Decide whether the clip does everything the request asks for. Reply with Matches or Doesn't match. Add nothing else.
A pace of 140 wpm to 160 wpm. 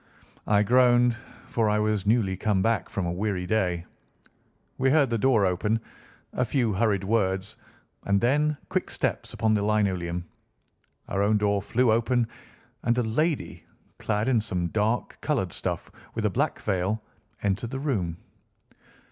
Matches